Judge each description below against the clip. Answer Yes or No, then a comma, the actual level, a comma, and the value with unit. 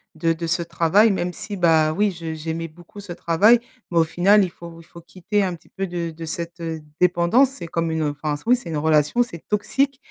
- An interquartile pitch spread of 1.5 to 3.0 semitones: No, average, 3.5 semitones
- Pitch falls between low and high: Yes, medium, 170 Hz